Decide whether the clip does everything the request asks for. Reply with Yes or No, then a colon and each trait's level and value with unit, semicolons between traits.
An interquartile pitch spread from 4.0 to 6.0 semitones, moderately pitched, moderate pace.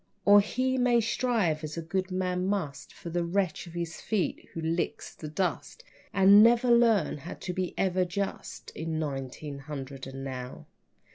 Yes: average, 4.7 semitones; medium, 180 Hz; average, 170 wpm